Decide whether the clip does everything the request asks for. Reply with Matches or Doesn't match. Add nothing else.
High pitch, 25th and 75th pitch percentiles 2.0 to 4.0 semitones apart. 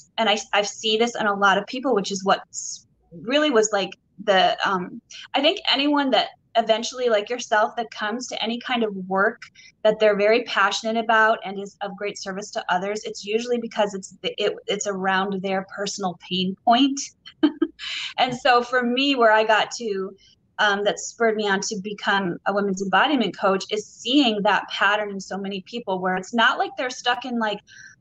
Matches